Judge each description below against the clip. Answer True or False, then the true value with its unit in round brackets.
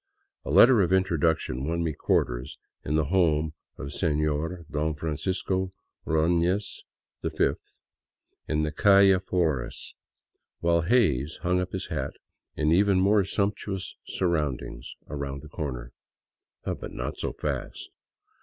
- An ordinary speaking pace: False (125 wpm)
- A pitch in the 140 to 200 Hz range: False (80 Hz)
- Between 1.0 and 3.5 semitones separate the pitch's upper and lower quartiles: False (3.9 semitones)